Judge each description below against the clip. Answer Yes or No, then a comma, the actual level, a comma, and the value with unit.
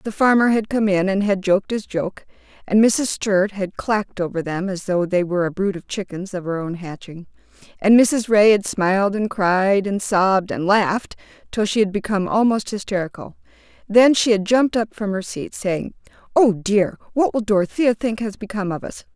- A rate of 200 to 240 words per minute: Yes, fast, 205 wpm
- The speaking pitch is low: No, high, 200 Hz